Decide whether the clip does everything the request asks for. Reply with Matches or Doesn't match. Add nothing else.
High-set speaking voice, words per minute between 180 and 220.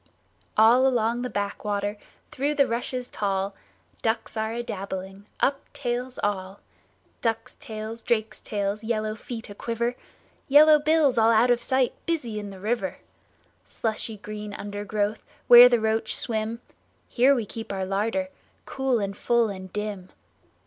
Doesn't match